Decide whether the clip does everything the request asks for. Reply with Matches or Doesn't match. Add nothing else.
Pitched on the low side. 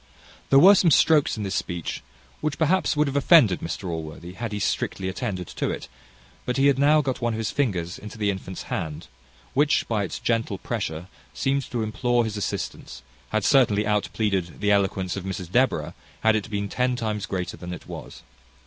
Matches